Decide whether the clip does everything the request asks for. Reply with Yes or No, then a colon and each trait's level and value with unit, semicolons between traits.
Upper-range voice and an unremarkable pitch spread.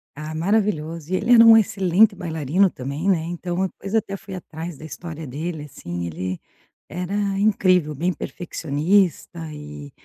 No: medium, 170 Hz; average, 4.3 semitones